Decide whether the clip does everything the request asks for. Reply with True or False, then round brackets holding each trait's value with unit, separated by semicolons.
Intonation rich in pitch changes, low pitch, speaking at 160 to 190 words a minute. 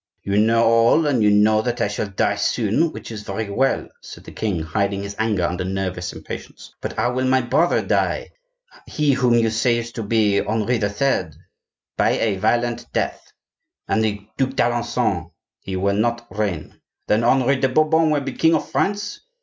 False (4.2 semitones; 115 Hz; 180 wpm)